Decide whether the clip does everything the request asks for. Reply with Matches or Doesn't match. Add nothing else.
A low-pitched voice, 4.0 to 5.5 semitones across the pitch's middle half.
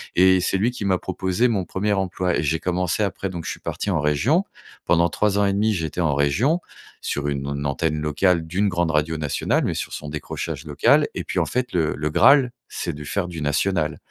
Matches